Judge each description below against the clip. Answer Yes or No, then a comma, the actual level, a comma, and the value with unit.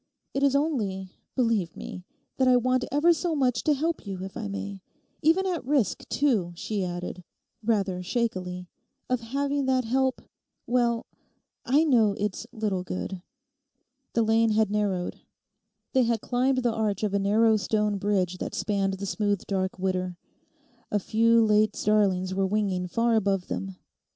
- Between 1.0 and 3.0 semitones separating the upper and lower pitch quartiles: No, average, 4.7 semitones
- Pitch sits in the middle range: No, high, 215 Hz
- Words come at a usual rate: Yes, average, 150 wpm